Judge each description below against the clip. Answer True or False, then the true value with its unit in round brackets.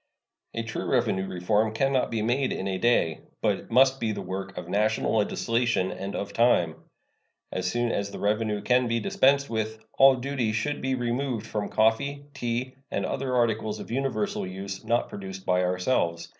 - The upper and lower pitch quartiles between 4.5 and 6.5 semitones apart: False (4.1 semitones)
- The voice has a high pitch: False (110 Hz)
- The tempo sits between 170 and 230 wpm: True (180 wpm)